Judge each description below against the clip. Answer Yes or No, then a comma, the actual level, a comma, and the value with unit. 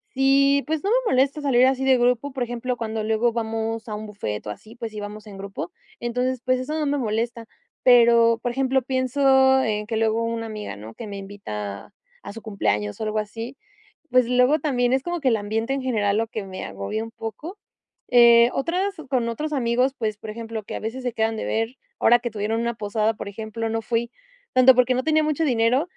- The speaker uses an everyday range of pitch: Yes, average, 3.1 semitones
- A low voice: No, high, 235 Hz